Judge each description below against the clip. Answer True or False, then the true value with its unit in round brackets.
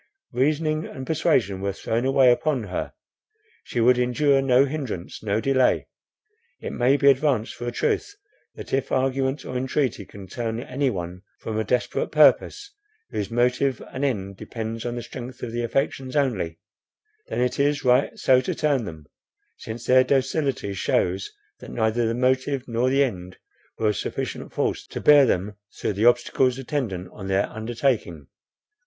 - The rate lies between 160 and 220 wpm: True (165 wpm)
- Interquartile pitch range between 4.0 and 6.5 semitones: False (3.6 semitones)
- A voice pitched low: True (125 Hz)